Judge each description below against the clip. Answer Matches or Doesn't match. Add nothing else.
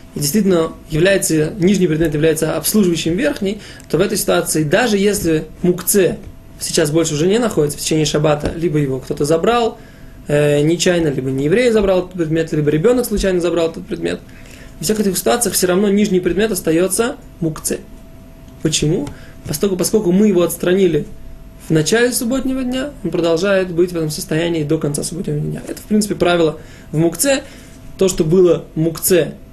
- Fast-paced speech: Matches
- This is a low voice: Doesn't match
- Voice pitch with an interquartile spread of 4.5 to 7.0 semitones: Doesn't match